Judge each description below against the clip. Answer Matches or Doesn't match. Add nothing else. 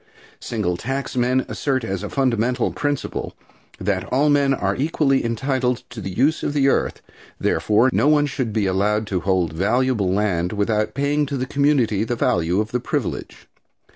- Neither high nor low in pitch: Doesn't match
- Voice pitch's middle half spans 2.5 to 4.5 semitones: Doesn't match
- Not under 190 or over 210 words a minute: Doesn't match